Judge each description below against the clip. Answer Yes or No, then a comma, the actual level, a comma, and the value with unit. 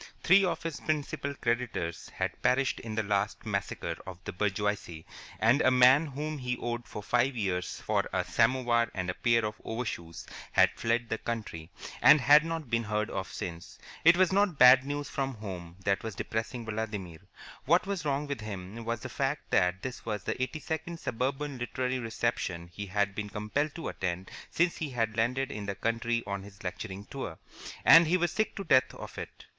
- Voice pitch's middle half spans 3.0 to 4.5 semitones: No, average, 5.2 semitones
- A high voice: No, low, 115 Hz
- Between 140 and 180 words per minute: No, average, 195 wpm